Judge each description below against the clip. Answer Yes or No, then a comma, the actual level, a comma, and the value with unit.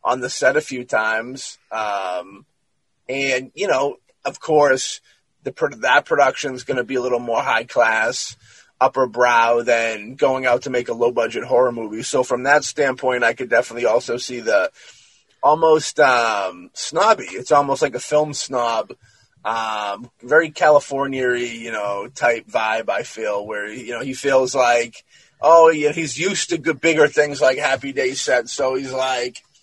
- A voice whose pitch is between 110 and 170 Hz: Yes, low, 135 Hz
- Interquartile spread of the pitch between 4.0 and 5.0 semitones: Yes, average, 4.4 semitones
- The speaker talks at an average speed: Yes, average, 175 wpm